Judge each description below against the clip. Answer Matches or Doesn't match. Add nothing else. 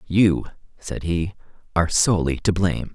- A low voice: Matches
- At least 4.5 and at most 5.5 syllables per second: Matches